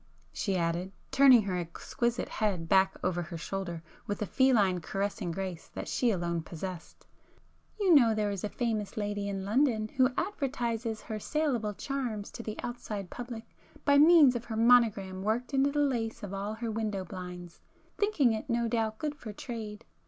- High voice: Yes, high, 215 Hz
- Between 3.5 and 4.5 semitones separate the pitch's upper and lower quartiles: Yes, average, 4.1 semitones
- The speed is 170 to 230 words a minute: Yes, average, 175 wpm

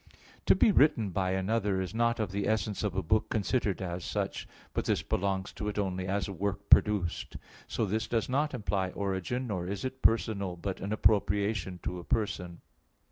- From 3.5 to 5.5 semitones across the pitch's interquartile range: No, narrow, 2.6 semitones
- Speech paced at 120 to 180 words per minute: No, average, 190 wpm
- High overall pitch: No, low, 100 Hz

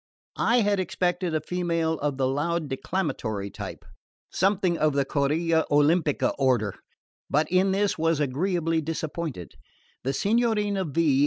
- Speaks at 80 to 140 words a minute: Yes, slow, 135 wpm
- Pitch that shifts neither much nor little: Yes, average, 4.3 semitones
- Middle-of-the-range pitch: Yes, medium, 165 Hz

